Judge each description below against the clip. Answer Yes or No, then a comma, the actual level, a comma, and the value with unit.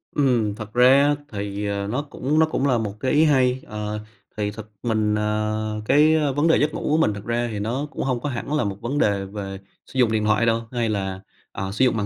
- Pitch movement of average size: Yes, average, 4.2 semitones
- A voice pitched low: Yes, low, 110 Hz